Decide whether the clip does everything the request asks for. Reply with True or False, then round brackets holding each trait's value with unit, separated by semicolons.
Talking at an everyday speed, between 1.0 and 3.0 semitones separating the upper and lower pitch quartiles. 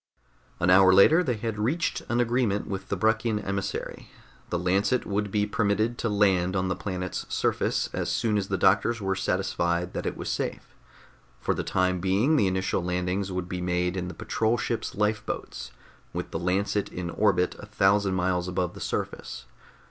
True (180 wpm; 2.6 semitones)